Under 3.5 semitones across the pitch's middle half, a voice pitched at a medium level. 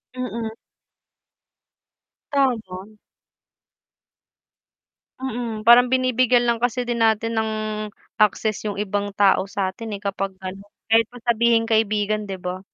No: average, 2.8 semitones; high, 220 Hz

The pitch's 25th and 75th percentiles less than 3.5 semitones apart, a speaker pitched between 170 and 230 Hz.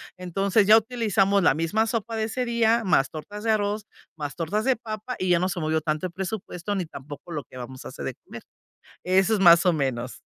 No: average, 5.1 semitones; high, 190 Hz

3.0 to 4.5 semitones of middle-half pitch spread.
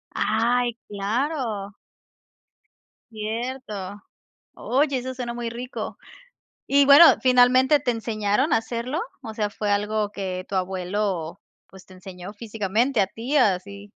Yes: average, 3.8 semitones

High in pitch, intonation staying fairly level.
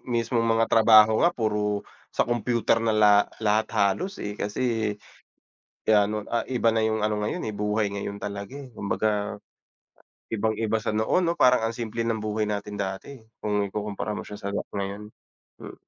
No: low, 110 Hz; narrow, 1.7 semitones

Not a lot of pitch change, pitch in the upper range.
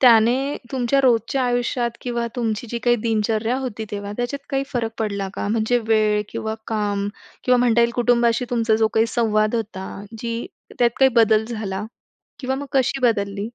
Yes: narrow, 2.2 semitones; high, 230 Hz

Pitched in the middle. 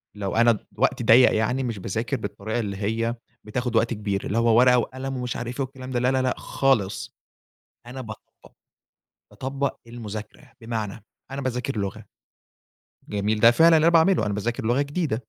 No: low, 120 Hz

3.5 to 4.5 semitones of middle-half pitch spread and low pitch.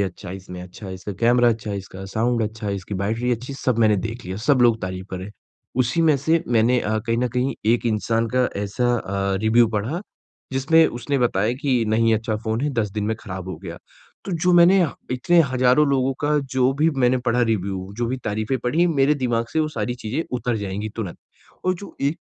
Yes: average, 4.1 semitones; low, 115 Hz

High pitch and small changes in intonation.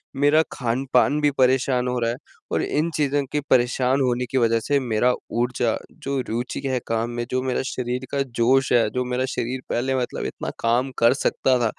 No: low, 125 Hz; narrow, 1.9 semitones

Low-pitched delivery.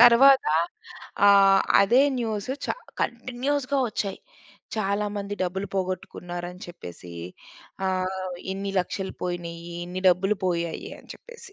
No: high, 195 Hz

